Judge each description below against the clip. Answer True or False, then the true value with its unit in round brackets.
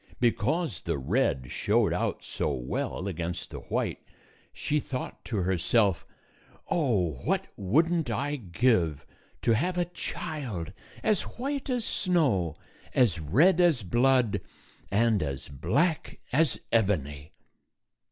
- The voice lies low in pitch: True (115 Hz)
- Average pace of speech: False (130 wpm)